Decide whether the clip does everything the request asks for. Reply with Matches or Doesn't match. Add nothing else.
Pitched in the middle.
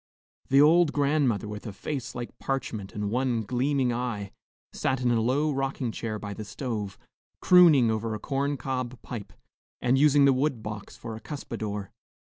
Doesn't match